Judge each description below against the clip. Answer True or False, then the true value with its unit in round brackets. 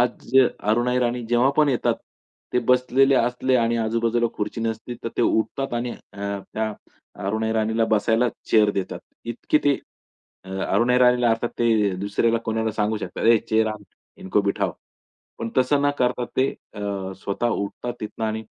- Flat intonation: True (2.2 semitones)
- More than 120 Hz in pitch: False (115 Hz)